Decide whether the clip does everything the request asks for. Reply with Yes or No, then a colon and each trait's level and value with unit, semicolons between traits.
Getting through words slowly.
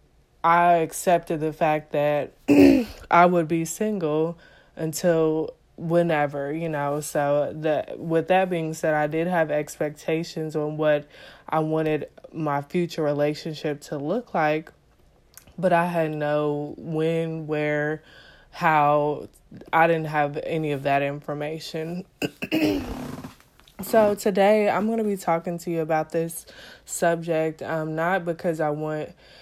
Yes: slow, 130 wpm